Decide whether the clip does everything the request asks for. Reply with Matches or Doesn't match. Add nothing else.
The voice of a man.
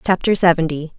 Doesn't match